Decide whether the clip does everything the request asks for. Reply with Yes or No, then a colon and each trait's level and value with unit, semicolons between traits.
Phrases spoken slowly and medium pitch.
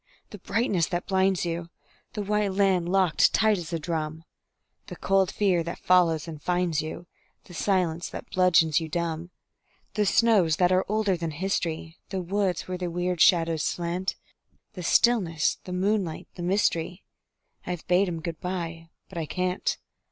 No: average, 165 wpm; medium, 180 Hz